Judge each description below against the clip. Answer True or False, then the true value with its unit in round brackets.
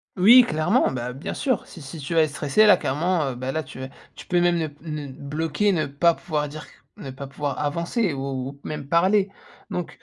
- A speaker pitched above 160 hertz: False (155 Hz)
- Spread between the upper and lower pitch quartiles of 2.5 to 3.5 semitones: False (4.0 semitones)